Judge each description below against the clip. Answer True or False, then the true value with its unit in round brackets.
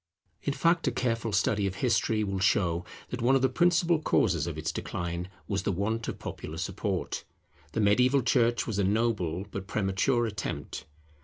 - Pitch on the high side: False (105 Hz)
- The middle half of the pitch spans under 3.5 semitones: False (4.2 semitones)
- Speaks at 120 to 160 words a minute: False (175 wpm)